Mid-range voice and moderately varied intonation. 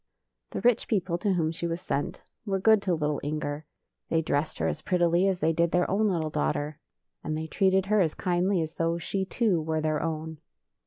Yes: medium, 170 Hz; average, 3.3 semitones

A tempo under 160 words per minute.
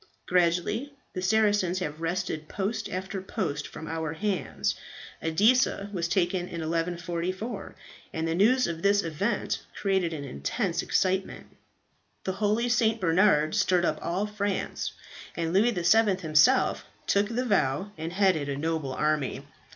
Yes: average, 140 wpm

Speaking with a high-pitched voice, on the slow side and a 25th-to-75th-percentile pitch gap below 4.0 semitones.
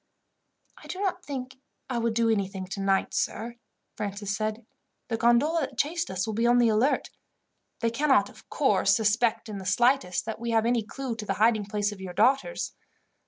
No: high, 230 Hz; average, 190 wpm; average, 3.4 semitones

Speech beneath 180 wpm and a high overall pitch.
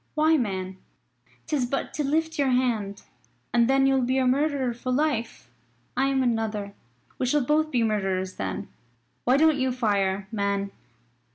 Yes: average, 160 wpm; very high, 250 Hz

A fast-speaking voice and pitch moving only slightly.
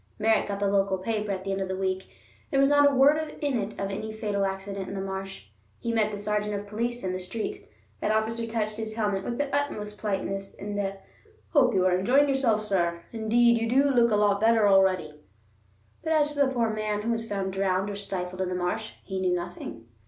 No: fast, 230 wpm; average, 3.2 semitones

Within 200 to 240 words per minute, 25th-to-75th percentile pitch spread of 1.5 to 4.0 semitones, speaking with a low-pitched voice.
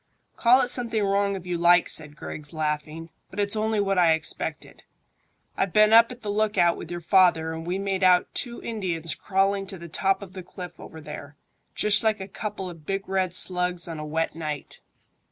No: fast, 205 wpm; average, 3.6 semitones; medium, 185 Hz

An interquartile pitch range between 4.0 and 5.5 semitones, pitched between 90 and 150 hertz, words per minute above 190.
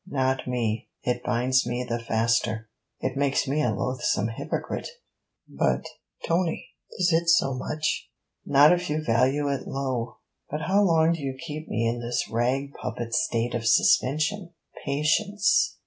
No: average, 4.5 semitones; low, 135 Hz; average, 150 wpm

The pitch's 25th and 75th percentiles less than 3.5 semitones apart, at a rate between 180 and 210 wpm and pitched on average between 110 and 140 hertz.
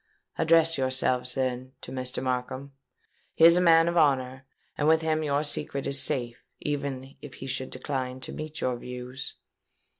No: average, 3.1 semitones; average, 170 wpm; low, 135 Hz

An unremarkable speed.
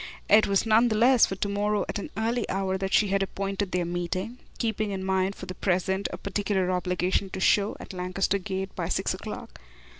No: fast, 215 wpm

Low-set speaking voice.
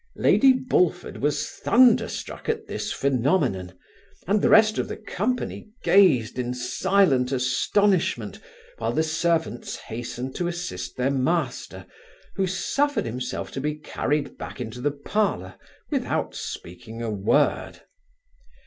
No: medium, 145 Hz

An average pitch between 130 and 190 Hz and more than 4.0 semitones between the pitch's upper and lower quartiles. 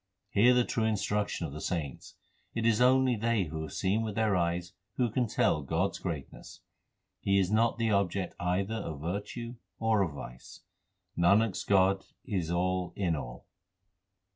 No: low, 100 Hz; average, 4.5 semitones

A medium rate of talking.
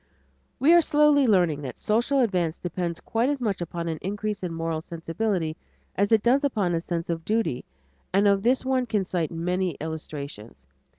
Yes: average, 180 wpm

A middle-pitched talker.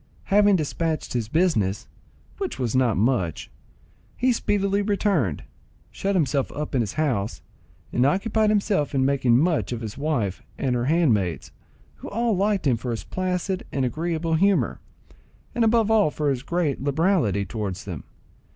Yes: medium, 150 Hz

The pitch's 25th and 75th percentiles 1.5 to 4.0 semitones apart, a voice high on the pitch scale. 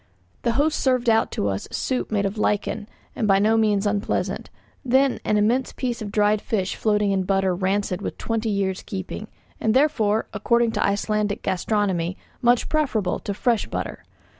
Yes: average, 2.7 semitones; high, 210 Hz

